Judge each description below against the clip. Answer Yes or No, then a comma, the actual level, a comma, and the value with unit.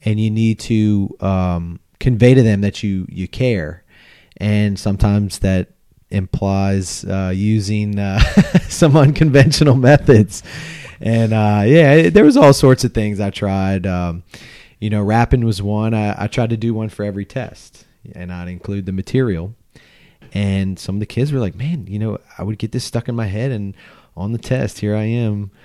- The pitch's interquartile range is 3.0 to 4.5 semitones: Yes, average, 3.3 semitones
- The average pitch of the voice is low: Yes, low, 105 Hz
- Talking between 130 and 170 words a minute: No, average, 180 wpm